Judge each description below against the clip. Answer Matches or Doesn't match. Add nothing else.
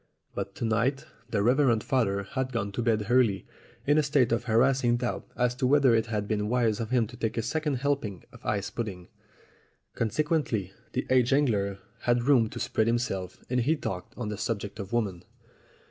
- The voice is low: Matches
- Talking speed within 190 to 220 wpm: Matches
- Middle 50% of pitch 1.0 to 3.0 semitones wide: Doesn't match